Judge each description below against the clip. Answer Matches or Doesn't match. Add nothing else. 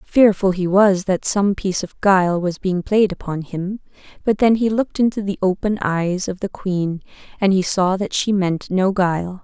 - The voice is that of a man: Doesn't match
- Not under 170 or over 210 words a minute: Matches